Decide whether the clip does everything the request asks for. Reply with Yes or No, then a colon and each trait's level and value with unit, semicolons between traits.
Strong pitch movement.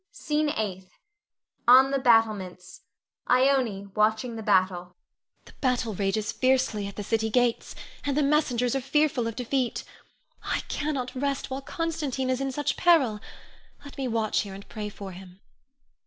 No: average, 4.5 semitones